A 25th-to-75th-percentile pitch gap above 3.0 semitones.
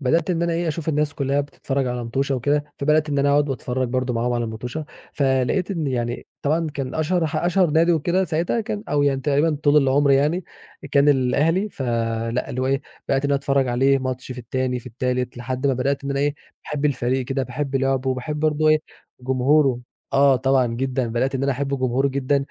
No: average, 2.7 semitones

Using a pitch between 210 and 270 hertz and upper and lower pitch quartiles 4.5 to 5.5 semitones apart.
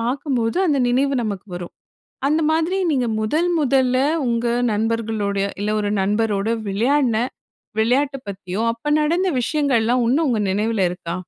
Yes: high, 235 Hz; average, 4.9 semitones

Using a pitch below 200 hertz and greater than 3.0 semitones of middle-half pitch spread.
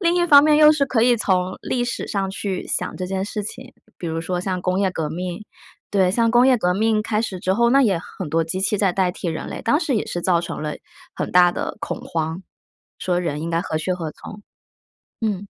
Yes: high, 190 Hz; average, 4.2 semitones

